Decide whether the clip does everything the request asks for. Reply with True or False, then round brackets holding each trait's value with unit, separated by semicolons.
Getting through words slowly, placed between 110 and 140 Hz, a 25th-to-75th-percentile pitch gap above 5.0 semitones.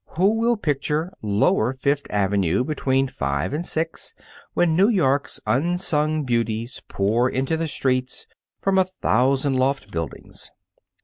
True (130 wpm; 135 Hz; 5.5 semitones)